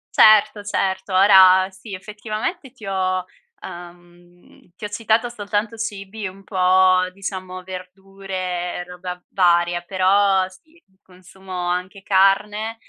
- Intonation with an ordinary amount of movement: No, narrow, 2.1 semitones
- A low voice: No, high, 190 Hz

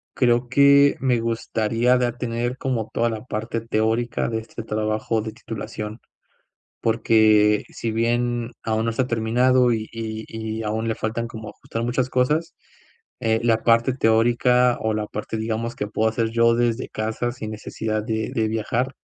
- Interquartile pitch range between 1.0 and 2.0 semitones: Yes, narrow, 1.6 semitones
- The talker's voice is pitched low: Yes, low, 115 Hz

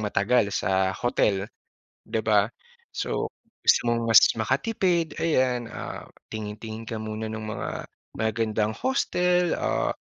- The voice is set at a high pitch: No, low, 110 Hz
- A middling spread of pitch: Yes, average, 3.2 semitones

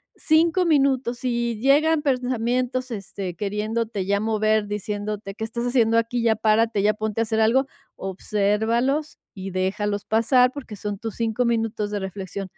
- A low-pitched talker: No, high, 225 Hz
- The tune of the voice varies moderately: Yes, average, 3.2 semitones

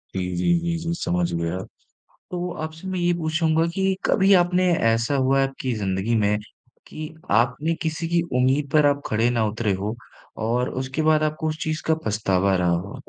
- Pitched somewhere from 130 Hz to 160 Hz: Yes, low, 135 Hz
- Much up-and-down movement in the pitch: Yes, wide, 7.2 semitones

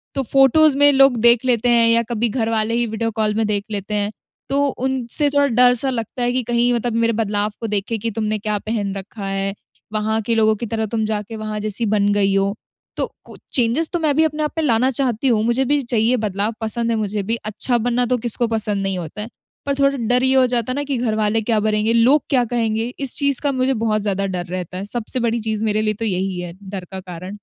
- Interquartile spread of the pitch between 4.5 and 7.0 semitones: No, average, 2.8 semitones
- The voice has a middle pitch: No, high, 225 Hz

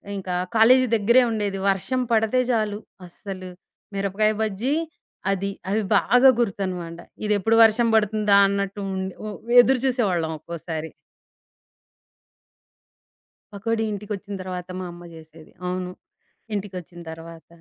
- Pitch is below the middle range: No, high, 200 Hz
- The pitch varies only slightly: No, average, 3.3 semitones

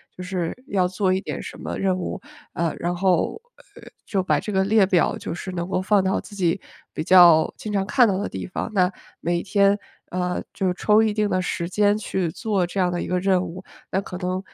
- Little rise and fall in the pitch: Yes, narrow, 1.9 semitones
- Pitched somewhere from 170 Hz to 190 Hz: Yes, medium, 185 Hz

